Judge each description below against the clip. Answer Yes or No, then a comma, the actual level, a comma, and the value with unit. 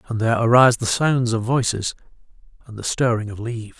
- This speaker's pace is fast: No, average, 190 wpm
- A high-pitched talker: No, low, 115 Hz